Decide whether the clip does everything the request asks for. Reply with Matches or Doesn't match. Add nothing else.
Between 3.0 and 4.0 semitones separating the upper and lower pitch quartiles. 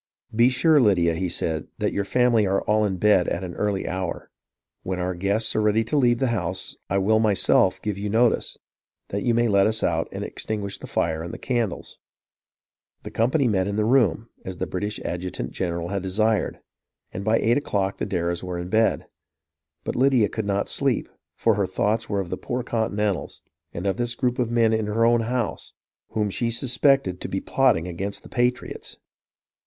Matches